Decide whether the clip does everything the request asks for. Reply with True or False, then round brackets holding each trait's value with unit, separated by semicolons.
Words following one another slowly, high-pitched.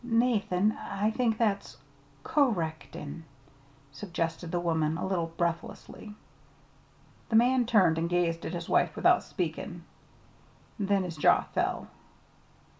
False (125 wpm; 180 Hz)